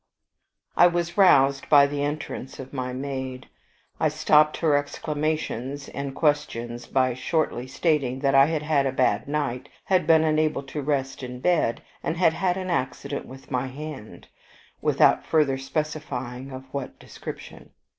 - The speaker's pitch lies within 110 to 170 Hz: Yes, medium, 140 Hz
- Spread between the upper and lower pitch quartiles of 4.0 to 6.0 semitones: No, average, 2.8 semitones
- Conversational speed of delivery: Yes, average, 155 wpm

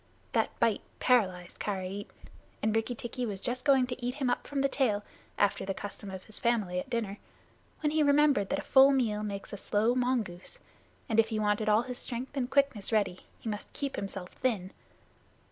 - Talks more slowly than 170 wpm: No, average, 195 wpm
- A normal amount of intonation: Yes, average, 4.1 semitones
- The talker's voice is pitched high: Yes, high, 225 Hz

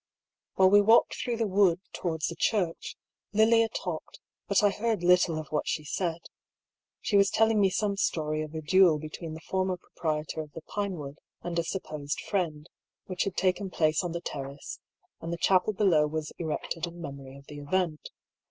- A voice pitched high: No, medium, 170 Hz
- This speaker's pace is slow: No, average, 185 wpm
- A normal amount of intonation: Yes, average, 4.0 semitones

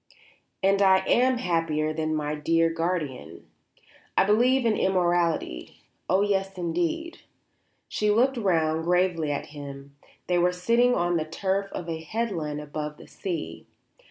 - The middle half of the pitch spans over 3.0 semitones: Yes, average, 4.1 semitones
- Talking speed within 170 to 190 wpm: No, average, 140 wpm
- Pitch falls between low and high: Yes, medium, 175 Hz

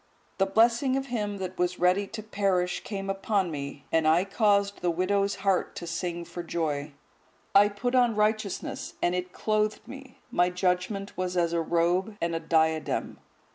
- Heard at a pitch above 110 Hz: Yes, high, 190 Hz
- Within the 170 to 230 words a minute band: Yes, average, 175 wpm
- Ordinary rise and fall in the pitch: Yes, average, 3.2 semitones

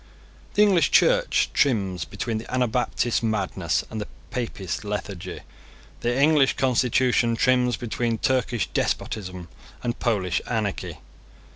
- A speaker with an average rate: No, slow, 115 wpm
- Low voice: Yes, low, 120 Hz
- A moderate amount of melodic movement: Yes, average, 3.6 semitones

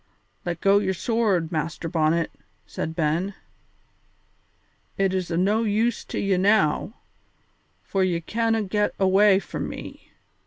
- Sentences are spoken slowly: Yes, slow, 130 wpm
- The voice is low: No, high, 190 Hz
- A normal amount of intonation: Yes, average, 3.6 semitones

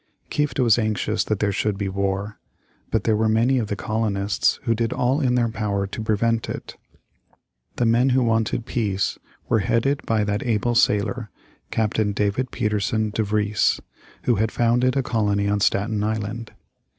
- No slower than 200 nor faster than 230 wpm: No, average, 170 wpm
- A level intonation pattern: Yes, narrow, 2.2 semitones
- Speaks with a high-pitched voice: No, low, 110 Hz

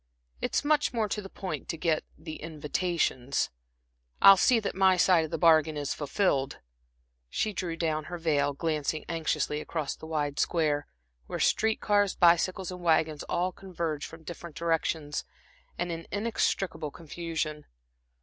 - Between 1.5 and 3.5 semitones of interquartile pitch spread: Yes, average, 3.1 semitones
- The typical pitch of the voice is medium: Yes, medium, 165 Hz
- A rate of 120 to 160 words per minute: Yes, average, 150 wpm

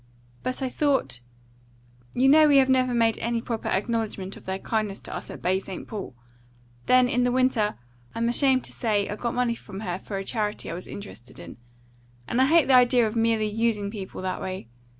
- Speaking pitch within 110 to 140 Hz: No, high, 230 Hz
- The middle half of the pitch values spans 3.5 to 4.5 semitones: Yes, average, 3.9 semitones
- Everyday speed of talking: No, fast, 210 wpm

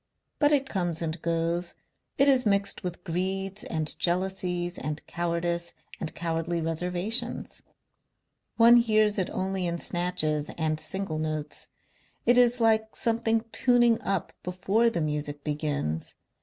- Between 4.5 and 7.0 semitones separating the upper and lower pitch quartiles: Yes, average, 4.9 semitones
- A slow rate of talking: Yes, slow, 130 wpm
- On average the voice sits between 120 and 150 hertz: No, medium, 180 Hz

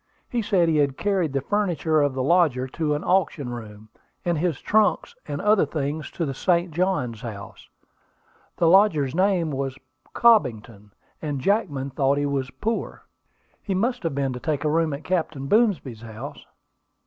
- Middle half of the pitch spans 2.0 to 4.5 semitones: No, wide, 5.6 semitones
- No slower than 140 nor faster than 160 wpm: No, average, 170 wpm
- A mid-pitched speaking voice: Yes, medium, 155 Hz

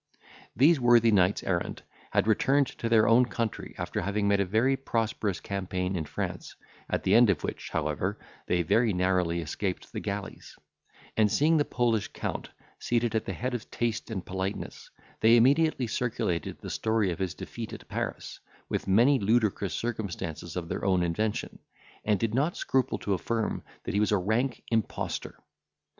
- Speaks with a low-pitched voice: Yes, low, 110 Hz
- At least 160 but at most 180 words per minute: Yes, average, 170 wpm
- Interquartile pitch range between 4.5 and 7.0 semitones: No, average, 3.9 semitones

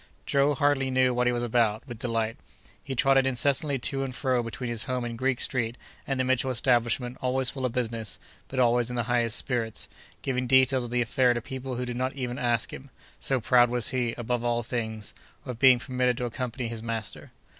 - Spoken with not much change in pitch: Yes, narrow, 1.7 semitones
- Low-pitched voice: Yes, low, 125 Hz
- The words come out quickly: Yes, fast, 210 wpm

